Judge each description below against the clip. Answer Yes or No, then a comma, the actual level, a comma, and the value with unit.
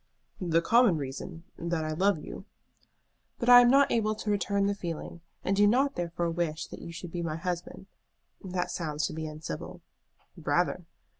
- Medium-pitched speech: Yes, medium, 175 Hz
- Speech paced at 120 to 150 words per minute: No, average, 175 wpm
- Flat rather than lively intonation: No, average, 3.8 semitones